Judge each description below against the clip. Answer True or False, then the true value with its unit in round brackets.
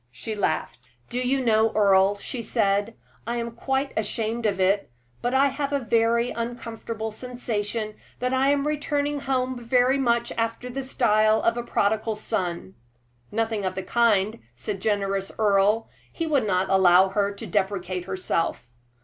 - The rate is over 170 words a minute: False (160 wpm)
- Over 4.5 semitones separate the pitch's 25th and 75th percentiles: False (3.7 semitones)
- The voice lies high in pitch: True (225 Hz)